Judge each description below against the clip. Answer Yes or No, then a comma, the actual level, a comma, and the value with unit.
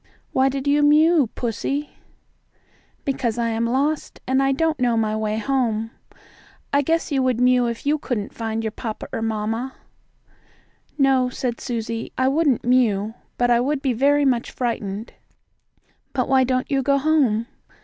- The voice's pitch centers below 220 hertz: No, very high, 255 Hz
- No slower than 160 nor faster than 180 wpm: Yes, average, 170 wpm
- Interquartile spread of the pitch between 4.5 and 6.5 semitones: No, average, 3.4 semitones